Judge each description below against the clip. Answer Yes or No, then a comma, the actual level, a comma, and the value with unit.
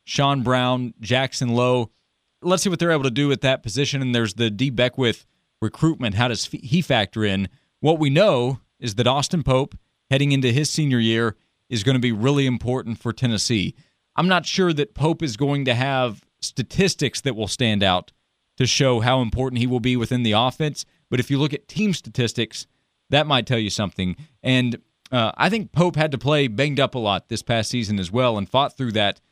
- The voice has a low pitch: Yes, low, 125 Hz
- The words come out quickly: Yes, fast, 210 wpm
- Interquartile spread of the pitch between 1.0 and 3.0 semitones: No, average, 3.5 semitones